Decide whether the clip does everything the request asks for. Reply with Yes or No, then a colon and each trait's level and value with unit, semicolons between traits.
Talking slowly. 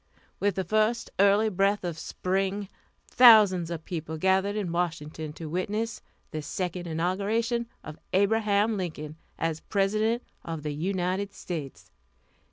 Yes: slow, 130 wpm